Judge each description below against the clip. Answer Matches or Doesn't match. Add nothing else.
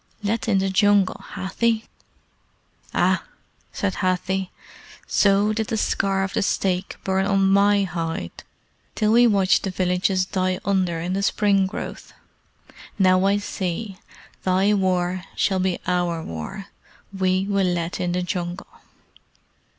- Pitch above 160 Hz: Matches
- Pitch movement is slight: Matches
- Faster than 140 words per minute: Doesn't match